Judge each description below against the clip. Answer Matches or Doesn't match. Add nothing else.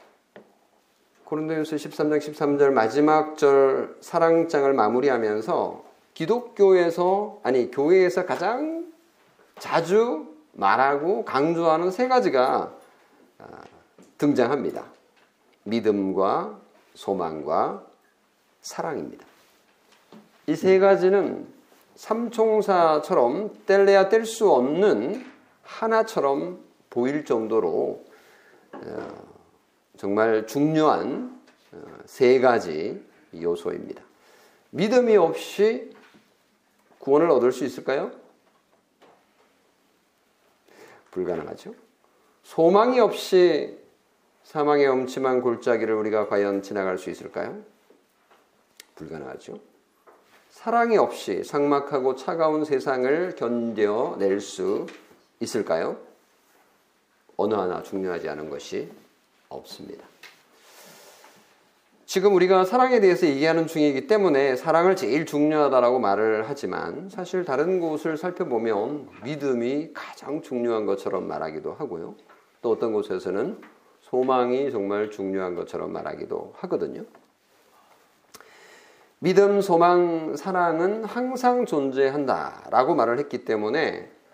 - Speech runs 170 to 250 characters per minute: Matches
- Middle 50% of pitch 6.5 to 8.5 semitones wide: Matches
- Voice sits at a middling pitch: Matches